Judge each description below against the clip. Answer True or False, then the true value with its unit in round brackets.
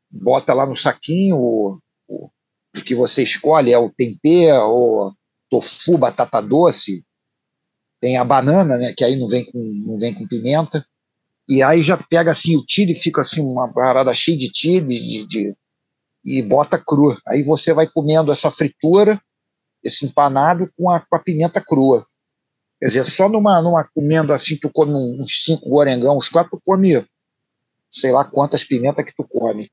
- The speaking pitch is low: False (150 Hz)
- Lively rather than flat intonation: False (4.4 semitones)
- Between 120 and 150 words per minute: False (175 wpm)